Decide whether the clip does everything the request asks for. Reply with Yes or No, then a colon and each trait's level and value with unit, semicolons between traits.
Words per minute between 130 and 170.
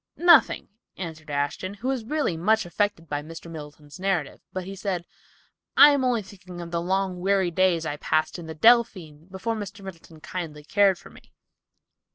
No: average, 180 wpm